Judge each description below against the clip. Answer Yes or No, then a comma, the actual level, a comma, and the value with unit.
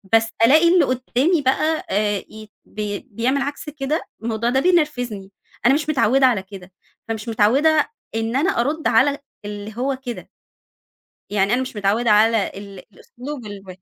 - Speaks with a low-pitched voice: No, high, 240 Hz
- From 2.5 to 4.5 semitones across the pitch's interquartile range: No, average, 5.2 semitones